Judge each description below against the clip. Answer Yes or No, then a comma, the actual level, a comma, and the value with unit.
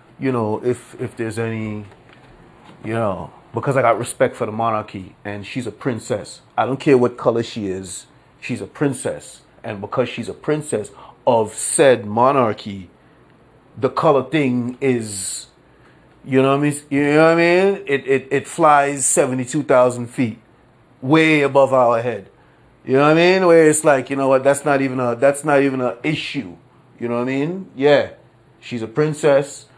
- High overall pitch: No, low, 135 Hz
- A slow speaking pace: No, average, 185 wpm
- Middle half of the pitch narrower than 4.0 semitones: Yes, average, 3.5 semitones